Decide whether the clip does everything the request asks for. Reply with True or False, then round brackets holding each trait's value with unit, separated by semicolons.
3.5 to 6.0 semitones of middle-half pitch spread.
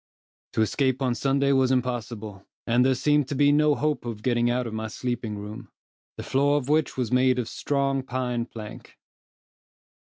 False (2.7 semitones)